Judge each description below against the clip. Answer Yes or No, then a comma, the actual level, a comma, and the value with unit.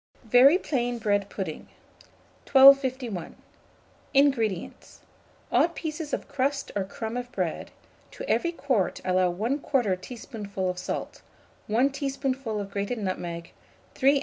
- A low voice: No, high, 240 Hz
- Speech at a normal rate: No, slow, 120 wpm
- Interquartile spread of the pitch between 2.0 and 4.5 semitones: No, wide, 5.6 semitones